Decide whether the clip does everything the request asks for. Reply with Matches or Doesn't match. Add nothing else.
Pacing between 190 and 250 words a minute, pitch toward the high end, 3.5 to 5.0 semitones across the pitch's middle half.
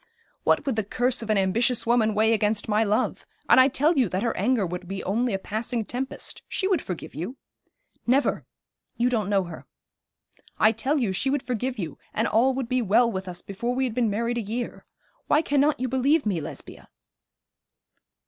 Matches